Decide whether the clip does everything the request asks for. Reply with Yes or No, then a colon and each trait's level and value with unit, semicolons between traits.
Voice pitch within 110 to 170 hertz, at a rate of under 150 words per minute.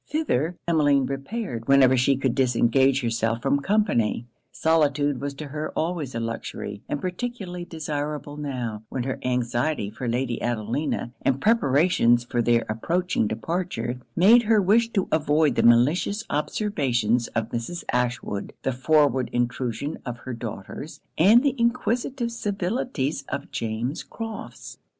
Yes: medium, 140 Hz; slow, 135 wpm